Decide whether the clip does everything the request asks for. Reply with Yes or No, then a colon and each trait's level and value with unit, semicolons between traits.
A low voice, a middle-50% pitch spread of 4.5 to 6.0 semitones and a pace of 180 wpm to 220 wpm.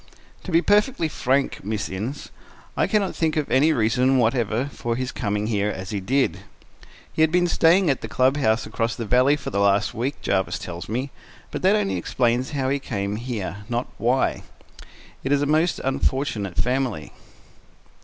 Yes: low, 125 Hz; average, 5.0 semitones; average, 185 wpm